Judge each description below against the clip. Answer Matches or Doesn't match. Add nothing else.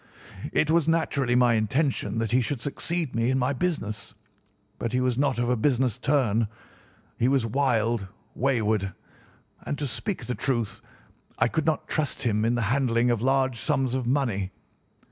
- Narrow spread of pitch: Doesn't match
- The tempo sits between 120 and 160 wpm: Doesn't match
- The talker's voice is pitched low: Matches